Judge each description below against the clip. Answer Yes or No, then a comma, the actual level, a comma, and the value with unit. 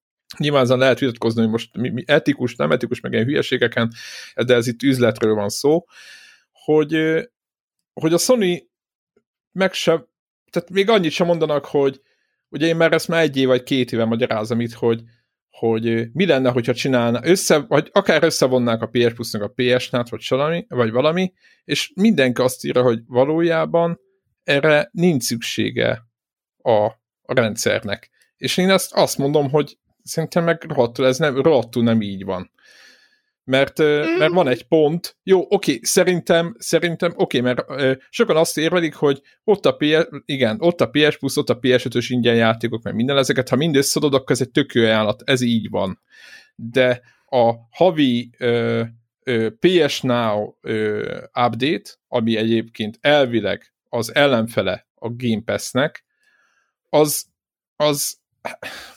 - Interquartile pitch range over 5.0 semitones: Yes, wide, 5.4 semitones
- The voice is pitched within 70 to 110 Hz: No, low, 130 Hz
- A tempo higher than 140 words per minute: Yes, fast, 155 wpm